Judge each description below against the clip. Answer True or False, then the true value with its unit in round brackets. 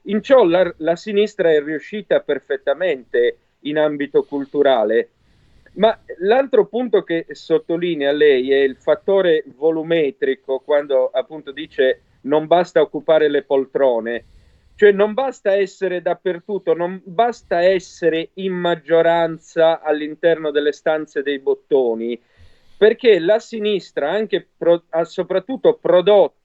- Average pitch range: False (5.7 semitones)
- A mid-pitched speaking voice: True (170 Hz)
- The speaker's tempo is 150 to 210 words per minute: False (115 wpm)